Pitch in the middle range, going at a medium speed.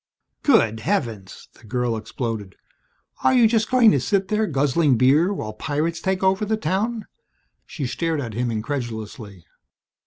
Yes: medium, 145 Hz; average, 150 wpm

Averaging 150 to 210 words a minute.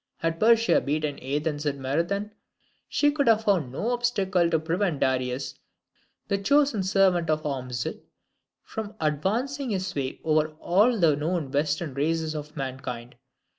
No: average, 140 wpm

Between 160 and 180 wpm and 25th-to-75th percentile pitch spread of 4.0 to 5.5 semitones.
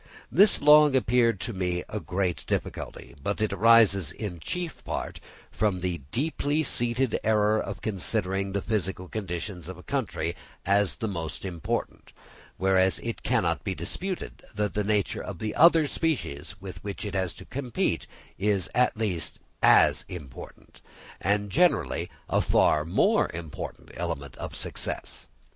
No: average, 150 wpm; average, 4.3 semitones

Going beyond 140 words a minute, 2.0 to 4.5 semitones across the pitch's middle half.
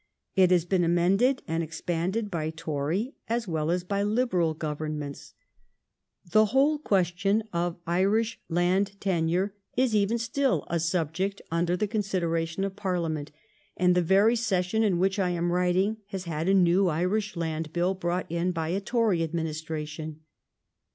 Yes: average, 155 wpm; average, 3.4 semitones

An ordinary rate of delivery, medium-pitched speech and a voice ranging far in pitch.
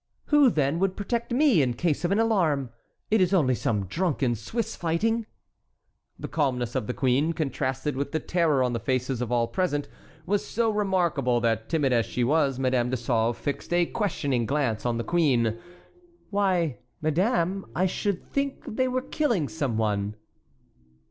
Yes: average, 170 wpm; medium, 150 Hz; wide, 7.4 semitones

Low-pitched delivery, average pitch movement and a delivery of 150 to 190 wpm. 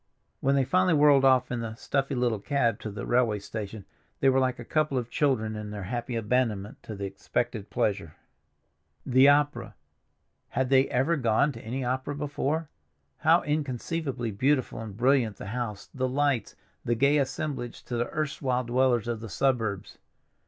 Yes: low, 125 Hz; average, 3.7 semitones; average, 165 wpm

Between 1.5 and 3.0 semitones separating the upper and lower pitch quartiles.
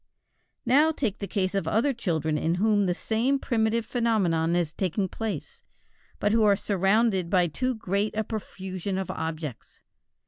No: average, 3.9 semitones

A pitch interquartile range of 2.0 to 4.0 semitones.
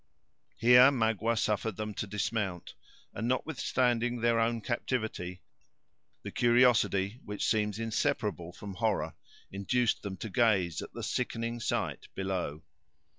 Yes: average, 3.2 semitones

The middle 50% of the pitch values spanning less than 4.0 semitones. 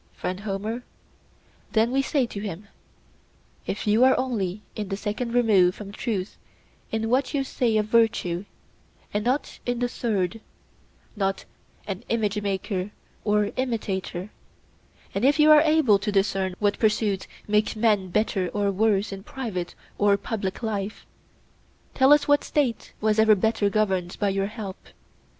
Yes: average, 3.0 semitones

